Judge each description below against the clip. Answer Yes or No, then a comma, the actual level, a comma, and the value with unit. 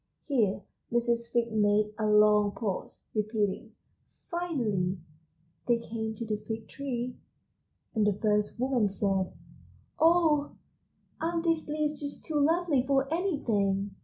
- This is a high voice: Yes, high, 230 Hz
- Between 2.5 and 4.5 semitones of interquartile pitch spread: No, wide, 5.5 semitones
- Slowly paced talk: Yes, slow, 125 wpm